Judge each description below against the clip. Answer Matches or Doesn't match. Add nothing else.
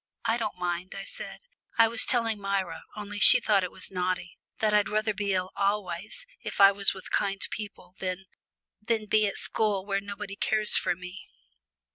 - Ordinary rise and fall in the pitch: Doesn't match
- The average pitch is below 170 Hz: Doesn't match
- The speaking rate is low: Doesn't match